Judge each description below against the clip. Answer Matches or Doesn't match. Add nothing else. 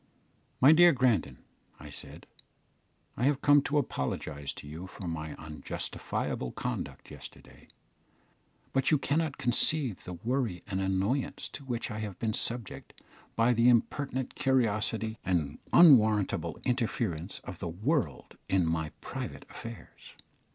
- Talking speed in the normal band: Doesn't match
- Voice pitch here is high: Doesn't match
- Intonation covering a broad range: Matches